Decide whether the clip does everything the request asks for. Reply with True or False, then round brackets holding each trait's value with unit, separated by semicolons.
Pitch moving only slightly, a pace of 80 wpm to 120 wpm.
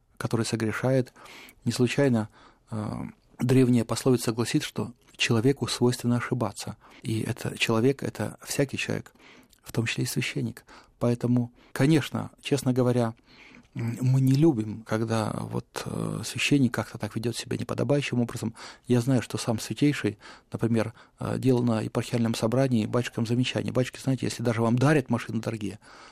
False (2.2 semitones; 140 wpm)